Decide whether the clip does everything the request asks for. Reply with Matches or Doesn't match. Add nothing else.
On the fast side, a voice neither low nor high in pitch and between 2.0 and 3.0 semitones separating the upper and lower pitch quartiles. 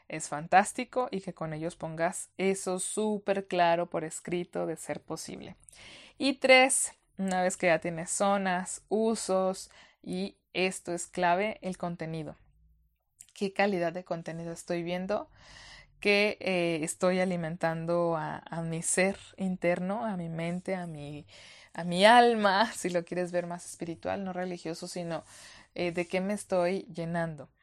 Doesn't match